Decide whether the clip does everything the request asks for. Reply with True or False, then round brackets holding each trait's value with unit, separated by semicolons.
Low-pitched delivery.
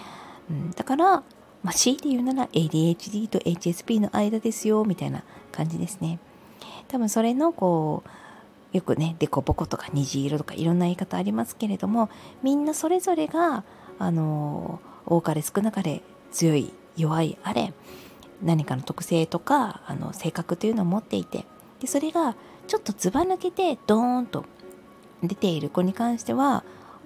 False (195 Hz)